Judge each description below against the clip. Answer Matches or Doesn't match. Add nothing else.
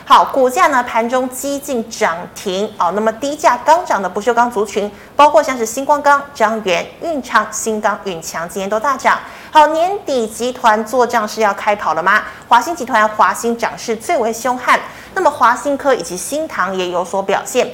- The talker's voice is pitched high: Matches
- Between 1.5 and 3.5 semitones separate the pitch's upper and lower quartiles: Doesn't match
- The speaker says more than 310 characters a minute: Doesn't match